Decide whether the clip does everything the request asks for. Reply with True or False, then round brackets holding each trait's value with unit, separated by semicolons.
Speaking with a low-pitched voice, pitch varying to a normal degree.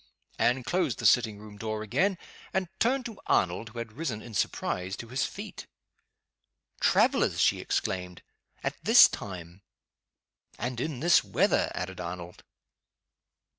False (110 Hz; 6.3 semitones)